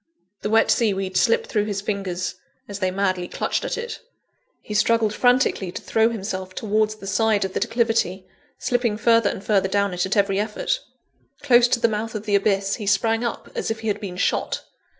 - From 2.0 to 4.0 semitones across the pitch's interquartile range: Yes, narrow, 2.6 semitones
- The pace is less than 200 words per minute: No, fast, 205 wpm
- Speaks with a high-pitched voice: Yes, high, 210 Hz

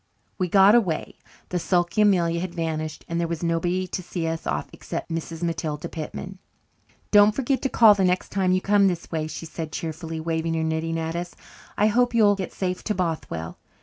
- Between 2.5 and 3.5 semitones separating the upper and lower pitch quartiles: Yes, average, 2.9 semitones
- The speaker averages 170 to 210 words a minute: Yes, average, 200 wpm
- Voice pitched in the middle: Yes, medium, 170 Hz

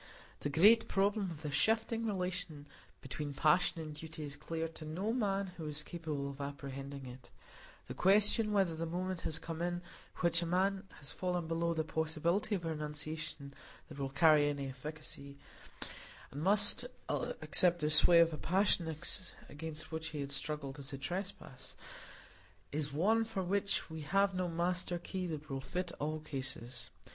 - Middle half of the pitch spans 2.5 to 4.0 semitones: Yes, average, 3.7 semitones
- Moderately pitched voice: Yes, medium, 160 Hz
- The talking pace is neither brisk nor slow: Yes, average, 170 wpm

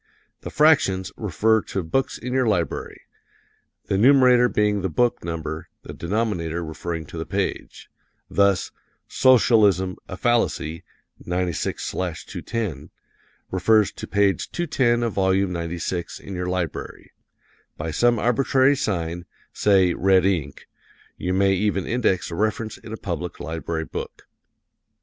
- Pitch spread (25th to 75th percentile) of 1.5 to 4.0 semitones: No, average, 4.5 semitones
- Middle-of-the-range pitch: No, very low, 95 Hz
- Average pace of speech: No, slow, 125 wpm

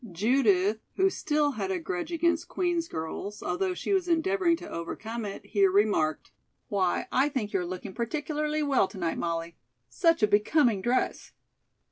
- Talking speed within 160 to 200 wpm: Yes, average, 165 wpm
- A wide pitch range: Yes, wide, 8.5 semitones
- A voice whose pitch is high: Yes, high, 220 Hz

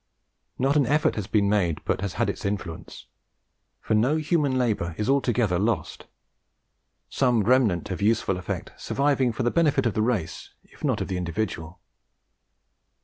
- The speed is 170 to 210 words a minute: No, average, 160 wpm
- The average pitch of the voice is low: Yes, low, 110 Hz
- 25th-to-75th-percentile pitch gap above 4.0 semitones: Yes, wide, 5.4 semitones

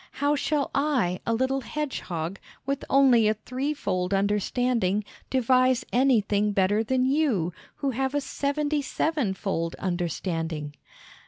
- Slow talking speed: Yes, slow, 115 wpm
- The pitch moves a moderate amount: No, wide, 6.1 semitones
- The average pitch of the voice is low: No, high, 240 Hz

